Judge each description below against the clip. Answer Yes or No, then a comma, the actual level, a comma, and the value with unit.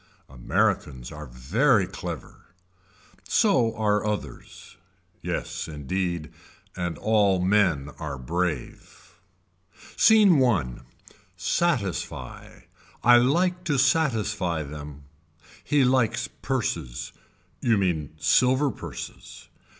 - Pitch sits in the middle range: No, very low, 95 Hz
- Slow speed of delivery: Yes, slow, 90 wpm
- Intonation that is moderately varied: No, wide, 8.7 semitones